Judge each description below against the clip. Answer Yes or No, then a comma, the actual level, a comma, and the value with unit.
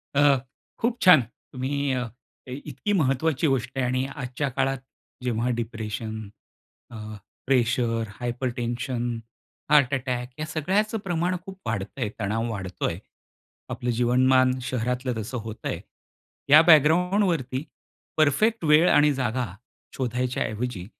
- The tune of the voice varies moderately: Yes, average, 3.7 semitones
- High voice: No, low, 130 Hz